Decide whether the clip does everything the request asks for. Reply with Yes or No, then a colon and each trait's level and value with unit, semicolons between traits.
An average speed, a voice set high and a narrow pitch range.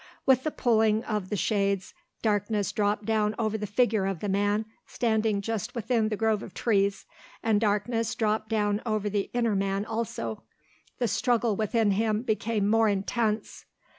Yes: average, 165 wpm; high, 215 Hz; narrow, 1.7 semitones